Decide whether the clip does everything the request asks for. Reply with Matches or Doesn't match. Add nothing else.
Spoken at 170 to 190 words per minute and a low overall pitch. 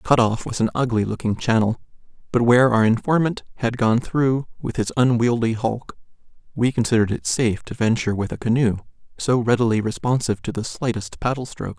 Matches